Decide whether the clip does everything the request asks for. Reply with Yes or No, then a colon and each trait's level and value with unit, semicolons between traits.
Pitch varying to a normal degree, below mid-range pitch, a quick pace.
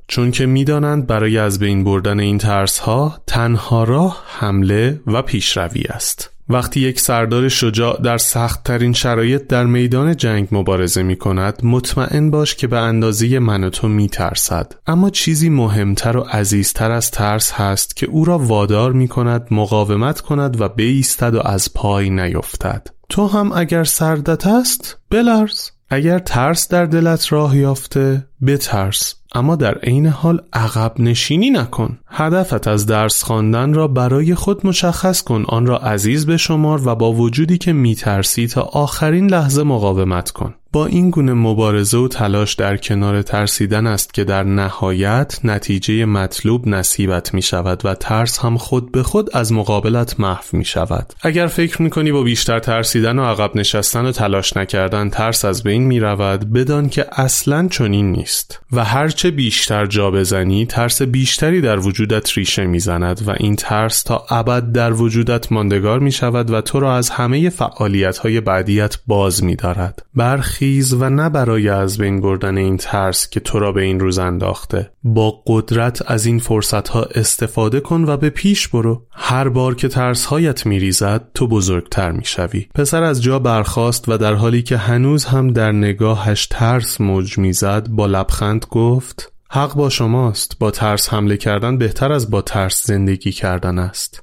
Yes: average, 4.7 semitones; low, 115 Hz; fast, 165 wpm